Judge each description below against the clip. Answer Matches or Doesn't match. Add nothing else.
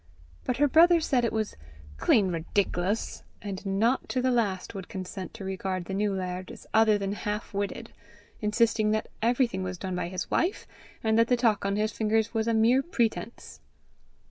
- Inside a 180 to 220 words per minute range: Matches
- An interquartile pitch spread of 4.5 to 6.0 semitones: Doesn't match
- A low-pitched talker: Doesn't match